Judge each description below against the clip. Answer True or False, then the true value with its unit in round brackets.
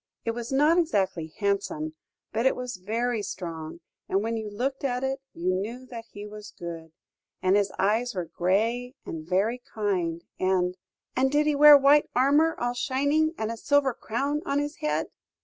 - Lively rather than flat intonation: True (6.1 semitones)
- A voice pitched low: False (230 Hz)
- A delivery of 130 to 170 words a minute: False (185 wpm)